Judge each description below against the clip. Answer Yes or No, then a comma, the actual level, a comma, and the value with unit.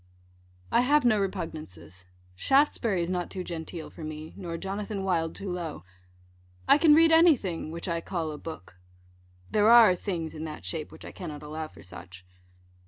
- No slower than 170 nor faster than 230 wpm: Yes, average, 175 wpm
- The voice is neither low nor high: Yes, medium, 175 Hz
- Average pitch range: Yes, average, 4.6 semitones